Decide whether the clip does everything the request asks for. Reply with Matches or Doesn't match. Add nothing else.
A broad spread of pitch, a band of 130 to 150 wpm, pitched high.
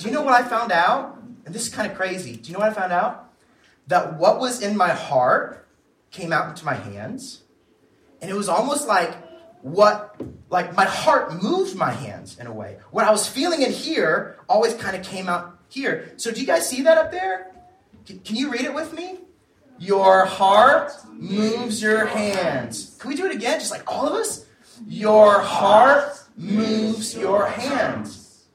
Doesn't match